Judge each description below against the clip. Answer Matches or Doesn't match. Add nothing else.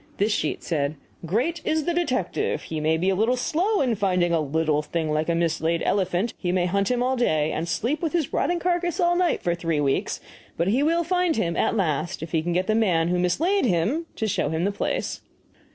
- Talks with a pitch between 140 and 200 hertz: Matches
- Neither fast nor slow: Doesn't match